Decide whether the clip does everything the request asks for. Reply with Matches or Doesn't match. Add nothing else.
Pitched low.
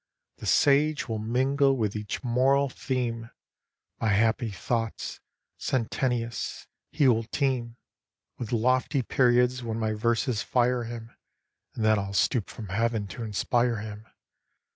Matches